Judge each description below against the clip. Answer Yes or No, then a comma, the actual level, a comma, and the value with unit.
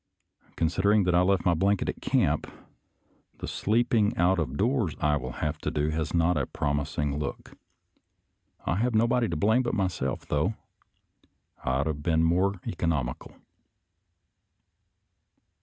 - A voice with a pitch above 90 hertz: No, very low, 85 Hz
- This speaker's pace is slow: No, average, 160 wpm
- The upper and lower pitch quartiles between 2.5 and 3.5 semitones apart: No, average, 5.1 semitones